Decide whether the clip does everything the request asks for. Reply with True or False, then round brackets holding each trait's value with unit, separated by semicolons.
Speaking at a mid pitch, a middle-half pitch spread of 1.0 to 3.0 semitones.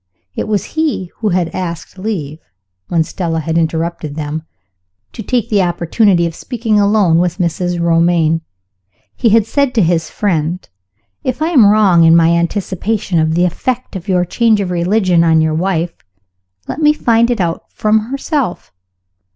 False (180 Hz; 4.5 semitones)